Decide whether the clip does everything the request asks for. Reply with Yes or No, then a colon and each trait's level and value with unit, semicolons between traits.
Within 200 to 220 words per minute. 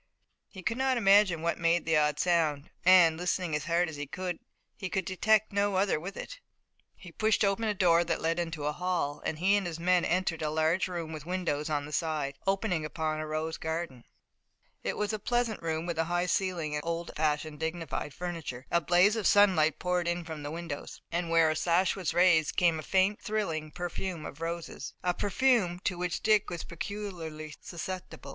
Yes: fast, 205 wpm